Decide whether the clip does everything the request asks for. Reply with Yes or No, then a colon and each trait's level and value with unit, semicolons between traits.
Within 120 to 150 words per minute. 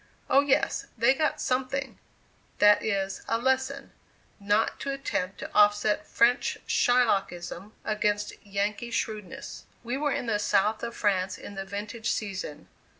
Yes: average, 140 wpm